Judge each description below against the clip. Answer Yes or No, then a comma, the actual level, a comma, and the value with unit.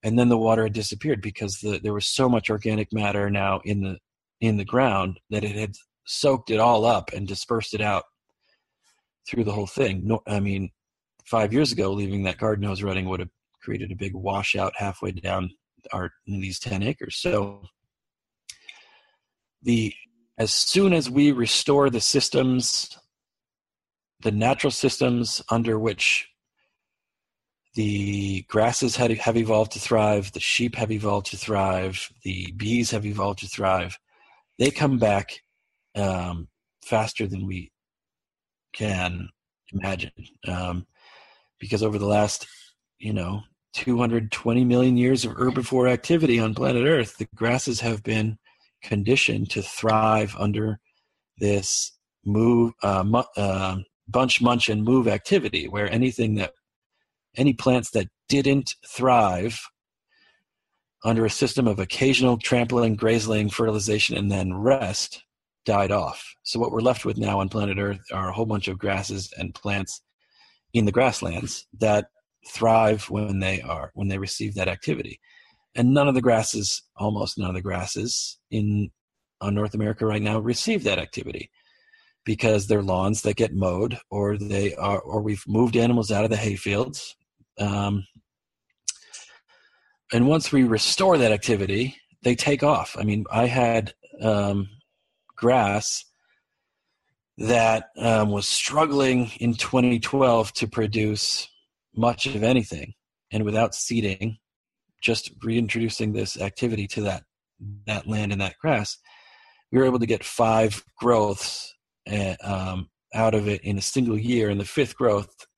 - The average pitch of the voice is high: No, low, 110 Hz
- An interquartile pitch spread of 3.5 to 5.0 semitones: No, average, 3.0 semitones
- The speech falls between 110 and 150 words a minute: Yes, average, 145 wpm